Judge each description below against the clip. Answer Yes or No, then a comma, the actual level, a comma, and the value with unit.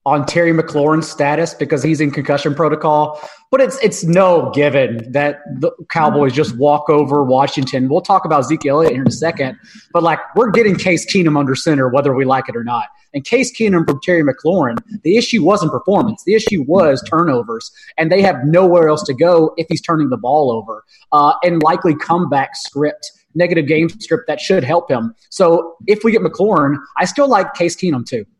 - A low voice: No, medium, 165 Hz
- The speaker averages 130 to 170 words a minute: No, average, 200 wpm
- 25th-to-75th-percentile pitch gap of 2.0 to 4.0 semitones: No, average, 4.4 semitones